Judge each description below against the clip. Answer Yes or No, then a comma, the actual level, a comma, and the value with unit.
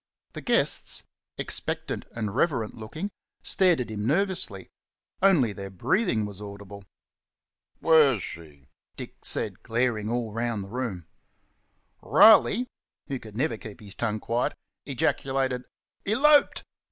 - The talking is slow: Yes, slow, 120 wpm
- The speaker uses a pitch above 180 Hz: No, low, 115 Hz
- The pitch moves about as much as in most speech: No, wide, 6.0 semitones